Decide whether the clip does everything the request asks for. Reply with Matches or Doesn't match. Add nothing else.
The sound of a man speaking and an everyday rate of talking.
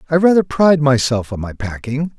Matches